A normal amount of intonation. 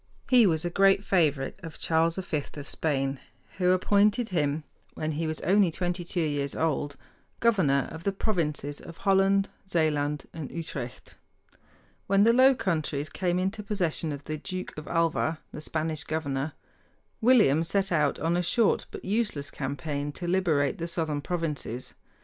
Yes: average, 4.4 semitones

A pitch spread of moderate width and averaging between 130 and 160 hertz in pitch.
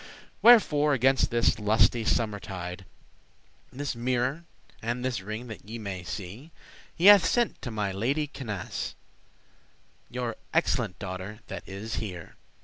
No: average, 4.7 semitones; low, 115 Hz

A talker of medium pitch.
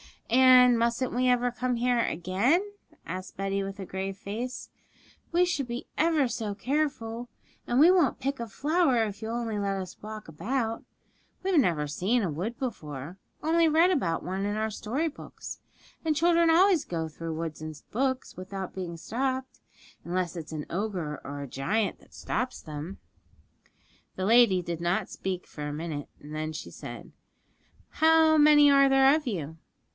No: high, 225 Hz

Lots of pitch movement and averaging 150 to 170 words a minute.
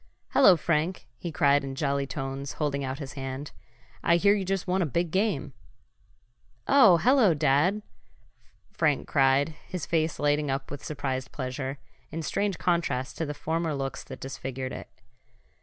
No: average, 4.2 semitones; average, 155 wpm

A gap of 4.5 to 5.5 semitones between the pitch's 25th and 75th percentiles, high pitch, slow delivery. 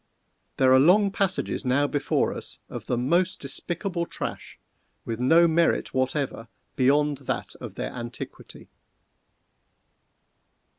No: average, 4.8 semitones; medium, 145 Hz; slow, 115 wpm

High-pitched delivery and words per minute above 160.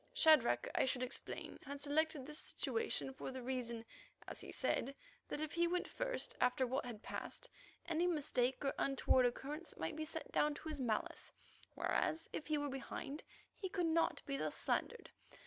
Yes: very high, 290 Hz; average, 180 wpm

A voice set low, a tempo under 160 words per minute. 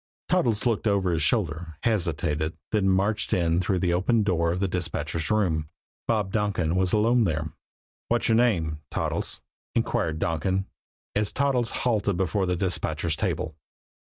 Yes: very low, 95 Hz; average, 150 wpm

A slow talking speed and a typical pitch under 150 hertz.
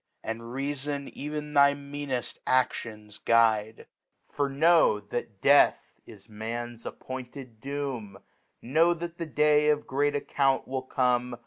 Yes: slow, 120 wpm; low, 135 Hz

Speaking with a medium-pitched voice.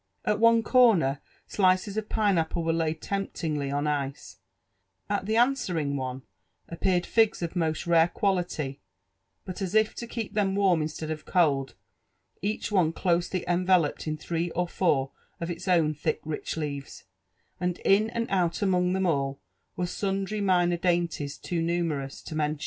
Yes: medium, 175 Hz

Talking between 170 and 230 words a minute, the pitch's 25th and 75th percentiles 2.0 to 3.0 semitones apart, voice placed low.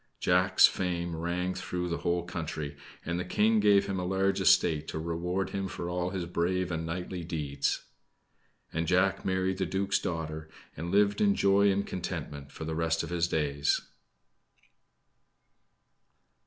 No: average, 155 wpm; narrow, 2.5 semitones; very low, 90 Hz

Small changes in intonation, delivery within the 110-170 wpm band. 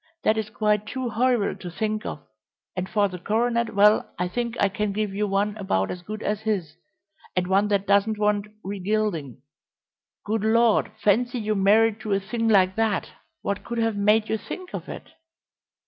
No: narrow, 2.0 semitones; average, 195 wpm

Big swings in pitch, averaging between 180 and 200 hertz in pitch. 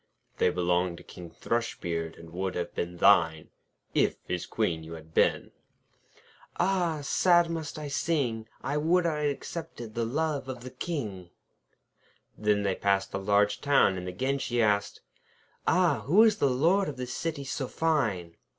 No: wide, 8.7 semitones; low, 120 Hz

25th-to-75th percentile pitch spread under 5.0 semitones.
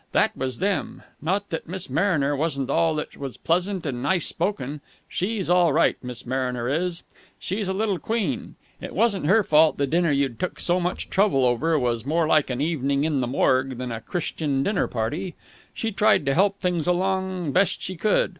No: wide, 5.6 semitones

